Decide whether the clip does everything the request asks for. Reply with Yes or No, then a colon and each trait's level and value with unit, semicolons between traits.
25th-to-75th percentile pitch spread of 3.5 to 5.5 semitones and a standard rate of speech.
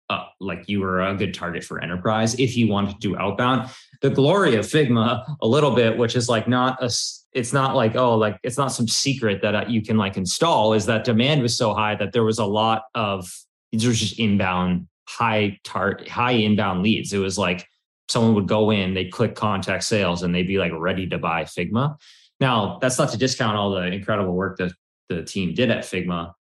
No: average, 4.0 semitones; fast, 220 wpm